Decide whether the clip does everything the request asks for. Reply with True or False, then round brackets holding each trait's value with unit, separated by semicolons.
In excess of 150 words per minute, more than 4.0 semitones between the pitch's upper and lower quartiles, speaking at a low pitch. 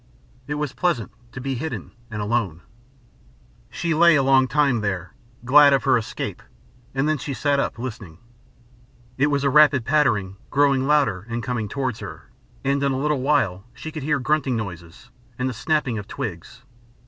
True (175 wpm; 4.6 semitones; 130 Hz)